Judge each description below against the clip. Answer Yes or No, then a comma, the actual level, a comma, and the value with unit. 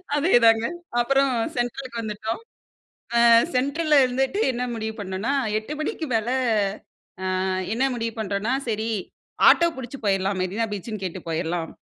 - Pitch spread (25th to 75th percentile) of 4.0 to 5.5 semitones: Yes, average, 4.5 semitones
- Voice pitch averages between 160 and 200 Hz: No, high, 230 Hz